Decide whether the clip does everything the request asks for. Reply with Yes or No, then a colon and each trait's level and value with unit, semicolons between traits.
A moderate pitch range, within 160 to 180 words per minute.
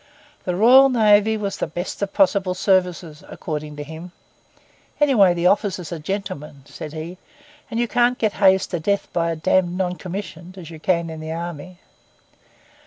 Yes: average, 3.4 semitones; average, 170 wpm